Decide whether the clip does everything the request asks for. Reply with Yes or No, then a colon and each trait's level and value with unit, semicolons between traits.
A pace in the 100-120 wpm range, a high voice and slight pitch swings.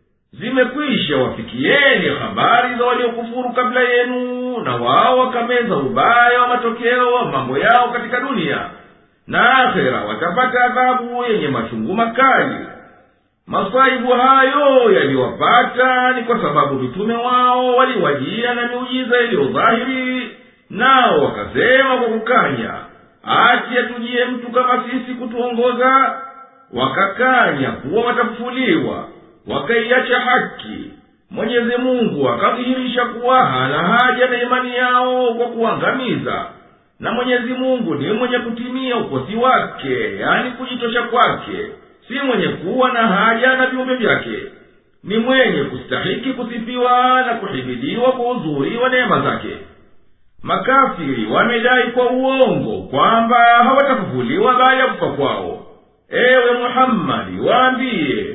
Yes: average, 105 wpm; high, 245 Hz; narrow, 1.3 semitones